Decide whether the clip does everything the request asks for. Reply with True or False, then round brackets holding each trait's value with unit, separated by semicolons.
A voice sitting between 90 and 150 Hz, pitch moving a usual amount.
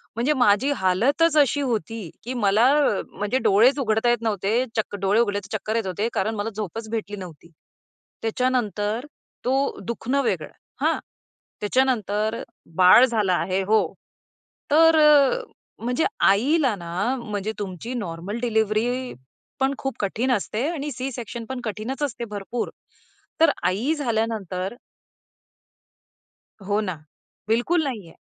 False (225 Hz; 3.8 semitones)